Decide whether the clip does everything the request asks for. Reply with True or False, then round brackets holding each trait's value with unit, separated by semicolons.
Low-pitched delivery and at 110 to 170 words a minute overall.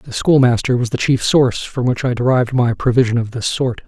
False (125 Hz; 230 wpm)